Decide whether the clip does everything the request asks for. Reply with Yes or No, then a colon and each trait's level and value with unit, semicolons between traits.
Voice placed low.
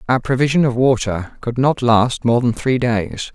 Yes: low, 120 Hz